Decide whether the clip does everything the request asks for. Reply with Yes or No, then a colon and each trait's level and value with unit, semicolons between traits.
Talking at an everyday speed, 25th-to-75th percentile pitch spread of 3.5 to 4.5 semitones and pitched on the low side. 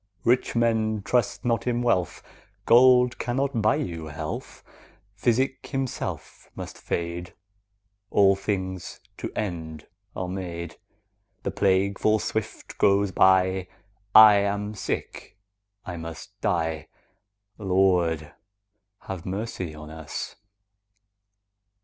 No: slow, 105 wpm; average, 4.1 semitones; very low, 95 Hz